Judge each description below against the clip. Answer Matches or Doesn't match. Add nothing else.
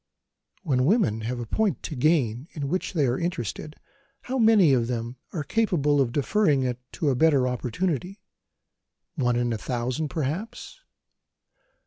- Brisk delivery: Doesn't match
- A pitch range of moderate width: Doesn't match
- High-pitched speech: Doesn't match